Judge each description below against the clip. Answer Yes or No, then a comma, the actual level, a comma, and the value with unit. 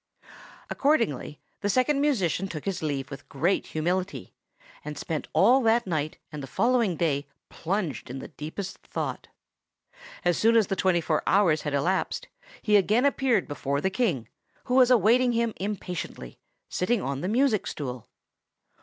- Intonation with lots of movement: Yes, wide, 7.3 semitones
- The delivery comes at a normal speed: Yes, average, 155 wpm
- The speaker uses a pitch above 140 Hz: Yes, medium, 185 Hz